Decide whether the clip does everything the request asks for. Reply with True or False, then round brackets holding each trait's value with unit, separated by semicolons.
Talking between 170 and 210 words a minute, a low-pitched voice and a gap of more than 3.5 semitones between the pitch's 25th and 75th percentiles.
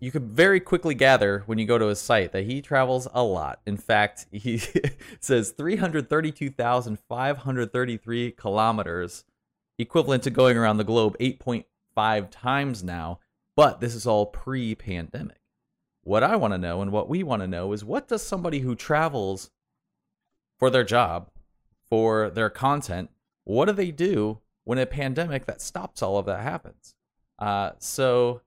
False (160 wpm; 120 Hz; 4.1 semitones)